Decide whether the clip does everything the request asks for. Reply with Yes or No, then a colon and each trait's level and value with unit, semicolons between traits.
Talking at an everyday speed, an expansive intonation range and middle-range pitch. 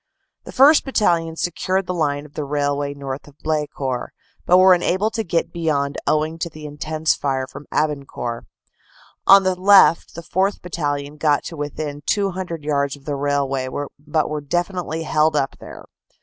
No: average, 165 wpm; average, 3.6 semitones; medium, 155 Hz